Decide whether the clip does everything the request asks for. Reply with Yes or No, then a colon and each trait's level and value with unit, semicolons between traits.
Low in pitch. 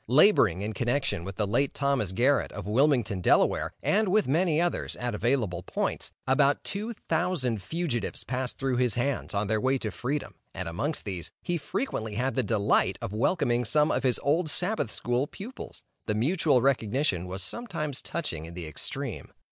Yes: low, 130 Hz